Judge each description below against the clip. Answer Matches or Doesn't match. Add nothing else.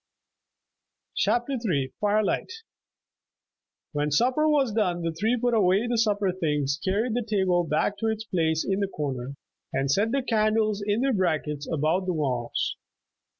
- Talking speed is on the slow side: Doesn't match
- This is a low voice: Doesn't match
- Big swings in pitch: Matches